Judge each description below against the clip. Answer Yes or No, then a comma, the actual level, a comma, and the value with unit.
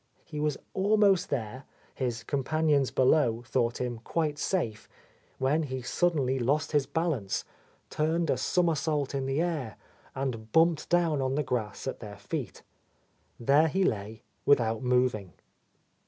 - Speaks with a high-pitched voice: No, low, 135 Hz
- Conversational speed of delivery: Yes, average, 150 wpm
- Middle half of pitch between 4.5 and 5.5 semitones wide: Yes, average, 4.8 semitones